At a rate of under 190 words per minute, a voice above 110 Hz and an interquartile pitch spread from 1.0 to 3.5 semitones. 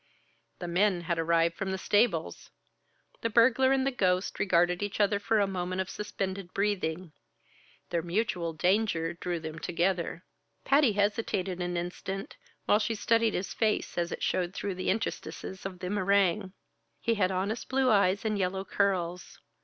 Yes: average, 160 wpm; high, 190 Hz; average, 2.9 semitones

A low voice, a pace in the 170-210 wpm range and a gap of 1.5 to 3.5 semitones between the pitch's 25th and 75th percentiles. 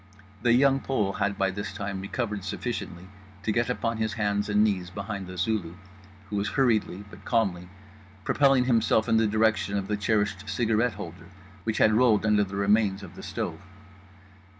Yes: low, 105 Hz; average, 175 wpm; narrow, 2.4 semitones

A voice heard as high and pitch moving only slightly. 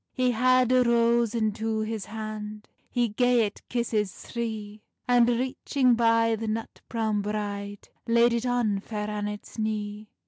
Yes: high, 225 Hz; narrow, 2.1 semitones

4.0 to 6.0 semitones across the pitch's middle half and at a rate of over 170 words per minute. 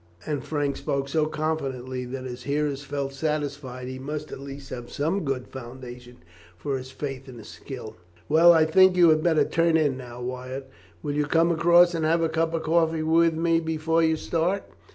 No: average, 3.6 semitones; average, 195 wpm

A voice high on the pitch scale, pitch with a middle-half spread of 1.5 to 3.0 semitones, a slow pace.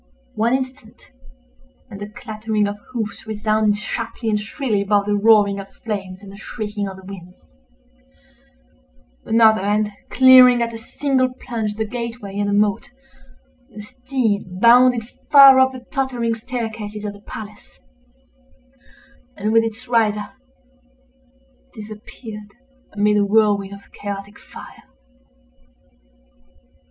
Yes: high, 215 Hz; narrow, 2.4 semitones; slow, 125 wpm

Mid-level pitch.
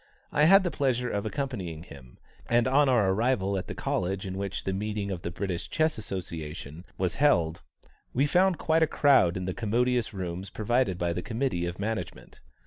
No: low, 100 Hz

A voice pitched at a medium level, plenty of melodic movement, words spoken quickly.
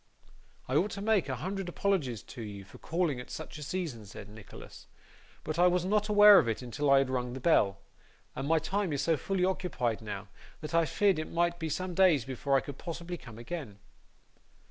Yes: medium, 155 Hz; wide, 6.5 semitones; fast, 210 wpm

